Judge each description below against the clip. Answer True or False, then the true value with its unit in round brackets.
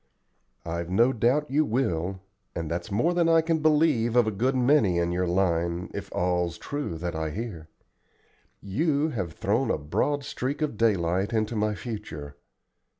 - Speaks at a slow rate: False (165 wpm)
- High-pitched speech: False (105 Hz)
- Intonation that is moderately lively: False (7.9 semitones)